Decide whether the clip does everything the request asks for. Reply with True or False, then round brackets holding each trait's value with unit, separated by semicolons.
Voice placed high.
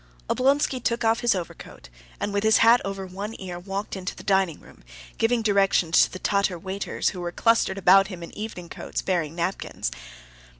True (195 Hz)